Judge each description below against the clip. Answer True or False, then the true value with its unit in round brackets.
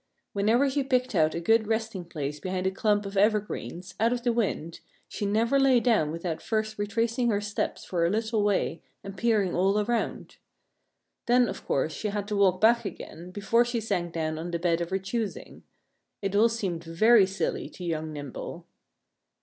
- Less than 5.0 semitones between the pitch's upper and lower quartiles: True (4.5 semitones)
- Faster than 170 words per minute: True (190 wpm)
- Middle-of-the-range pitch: False (205 Hz)